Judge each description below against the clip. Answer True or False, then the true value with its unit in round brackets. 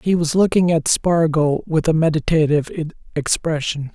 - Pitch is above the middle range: False (160 Hz)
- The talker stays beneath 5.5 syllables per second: True (4.7 syllables/s)